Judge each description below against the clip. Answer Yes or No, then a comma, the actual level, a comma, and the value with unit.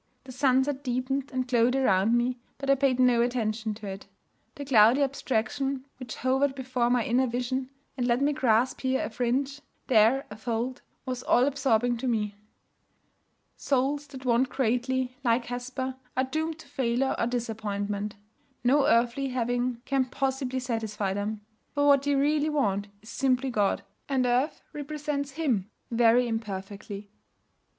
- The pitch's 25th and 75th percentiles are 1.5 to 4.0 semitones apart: Yes, average, 2.7 semitones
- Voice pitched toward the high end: Yes, very high, 250 Hz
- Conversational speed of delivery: Yes, average, 155 wpm